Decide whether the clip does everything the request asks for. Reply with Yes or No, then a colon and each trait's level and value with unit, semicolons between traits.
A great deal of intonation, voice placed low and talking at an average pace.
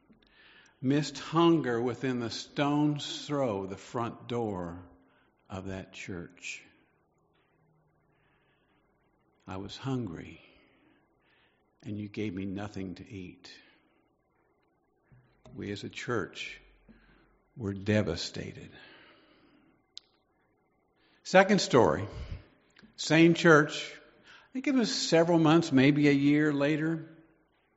No: wide, 7.5 semitones; low, 130 Hz; slow, 90 wpm